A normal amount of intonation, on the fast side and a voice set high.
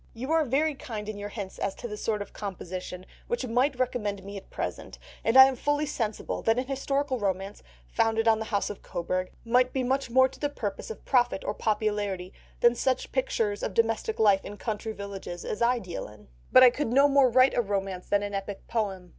Yes: average, 4.2 semitones; fast, 220 wpm; high, 220 Hz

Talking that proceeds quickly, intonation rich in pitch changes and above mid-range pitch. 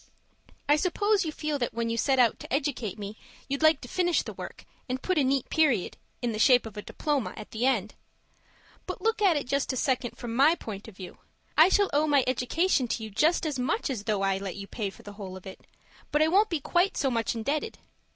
Yes: fast, 240 wpm; wide, 5.9 semitones; very high, 260 Hz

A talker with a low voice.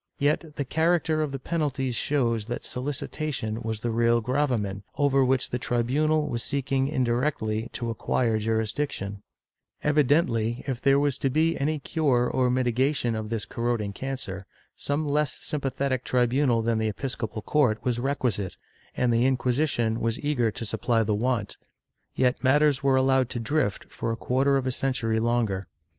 Yes: low, 125 Hz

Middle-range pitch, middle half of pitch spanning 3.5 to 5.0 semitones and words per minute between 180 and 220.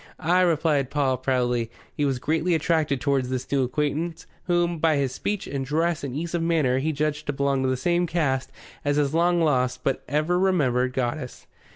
Yes: medium, 145 Hz; average, 4.0 semitones; average, 190 wpm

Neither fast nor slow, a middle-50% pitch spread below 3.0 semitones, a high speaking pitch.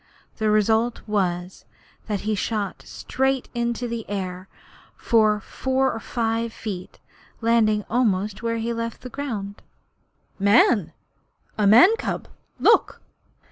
No: slow, 130 wpm; narrow, 2.5 semitones; high, 220 Hz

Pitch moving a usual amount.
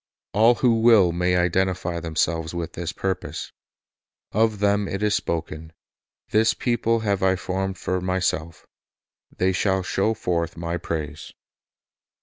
Yes: average, 3.4 semitones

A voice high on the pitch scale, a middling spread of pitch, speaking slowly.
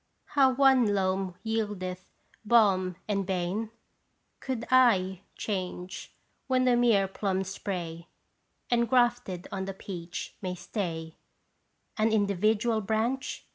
Yes: high, 200 Hz; average, 3.7 semitones; slow, 105 wpm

